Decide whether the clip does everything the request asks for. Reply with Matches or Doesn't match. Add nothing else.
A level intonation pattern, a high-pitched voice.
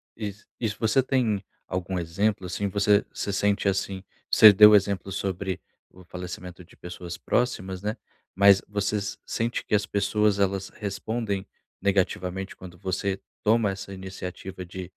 Doesn't match